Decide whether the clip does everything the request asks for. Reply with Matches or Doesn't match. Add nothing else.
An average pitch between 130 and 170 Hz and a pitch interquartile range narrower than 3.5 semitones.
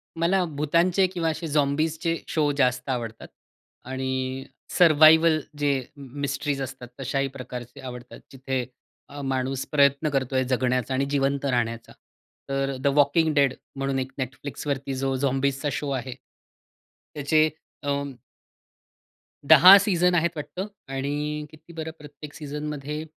Matches